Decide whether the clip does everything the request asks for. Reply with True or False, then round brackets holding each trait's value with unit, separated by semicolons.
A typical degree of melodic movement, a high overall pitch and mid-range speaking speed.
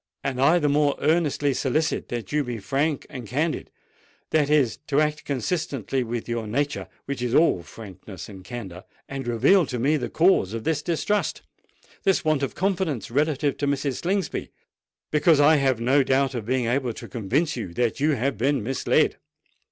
False (4.1 semitones; 135 Hz; 165 wpm)